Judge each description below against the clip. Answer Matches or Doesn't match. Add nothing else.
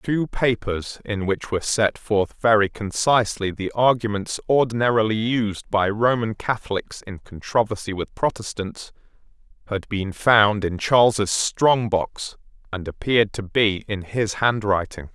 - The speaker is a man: Matches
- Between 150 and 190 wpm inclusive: Doesn't match